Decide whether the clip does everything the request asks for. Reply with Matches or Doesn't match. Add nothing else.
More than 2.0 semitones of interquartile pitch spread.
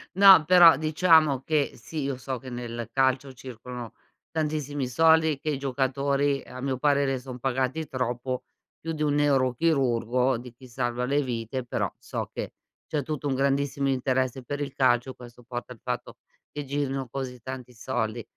Matches